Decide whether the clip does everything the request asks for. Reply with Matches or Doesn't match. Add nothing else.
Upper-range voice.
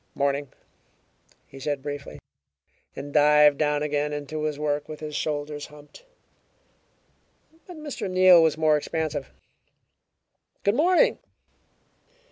Doesn't match